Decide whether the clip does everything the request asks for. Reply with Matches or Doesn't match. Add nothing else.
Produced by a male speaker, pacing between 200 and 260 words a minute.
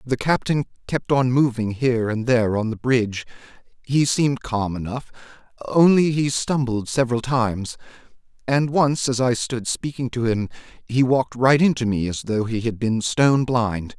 Doesn't match